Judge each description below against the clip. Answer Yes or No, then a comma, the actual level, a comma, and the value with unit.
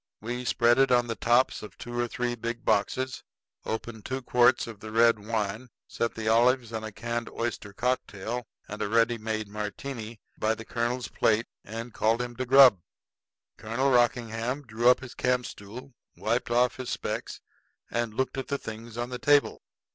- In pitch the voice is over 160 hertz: No, low, 120 Hz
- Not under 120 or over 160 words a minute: No, average, 180 wpm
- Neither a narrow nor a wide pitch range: No, narrow, 1.9 semitones